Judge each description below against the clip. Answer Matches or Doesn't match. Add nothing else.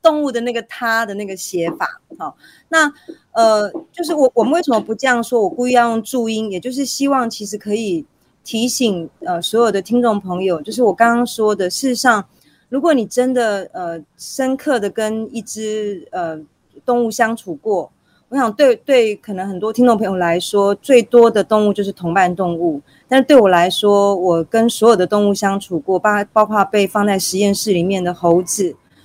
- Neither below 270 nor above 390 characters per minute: Matches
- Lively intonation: Doesn't match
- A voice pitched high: Matches